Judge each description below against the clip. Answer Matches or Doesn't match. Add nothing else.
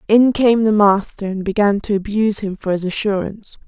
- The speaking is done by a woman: Matches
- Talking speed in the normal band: Matches